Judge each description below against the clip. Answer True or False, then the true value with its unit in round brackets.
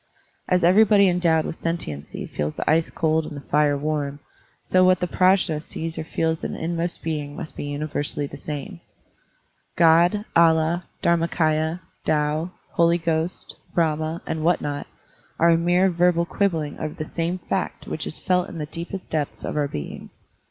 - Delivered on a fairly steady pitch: True (2.3 semitones)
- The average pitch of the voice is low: False (165 Hz)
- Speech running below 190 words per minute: True (175 wpm)